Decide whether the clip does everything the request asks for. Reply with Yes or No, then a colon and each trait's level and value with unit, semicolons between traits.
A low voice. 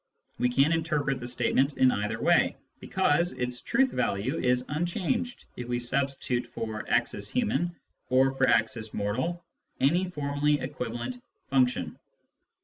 Yes: low, 130 Hz